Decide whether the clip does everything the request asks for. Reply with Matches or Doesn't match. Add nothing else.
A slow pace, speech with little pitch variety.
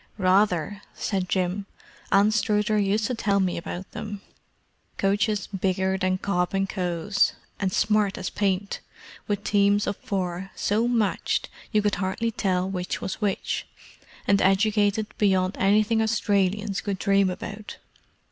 Matches